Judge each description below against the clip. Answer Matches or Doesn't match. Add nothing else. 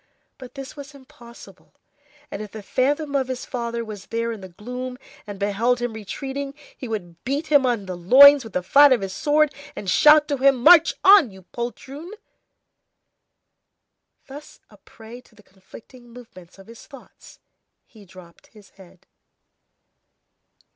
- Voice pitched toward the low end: Doesn't match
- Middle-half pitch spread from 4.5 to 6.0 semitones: Matches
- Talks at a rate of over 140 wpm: Matches